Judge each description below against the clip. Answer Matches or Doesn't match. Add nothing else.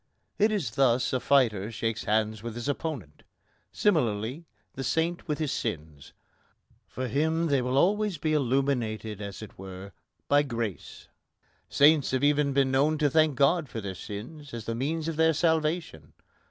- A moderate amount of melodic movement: Doesn't match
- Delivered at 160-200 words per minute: Matches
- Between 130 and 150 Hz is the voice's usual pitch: Matches